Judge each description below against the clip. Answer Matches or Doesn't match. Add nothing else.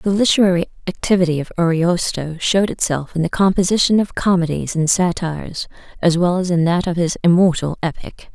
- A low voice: Doesn't match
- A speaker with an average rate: Matches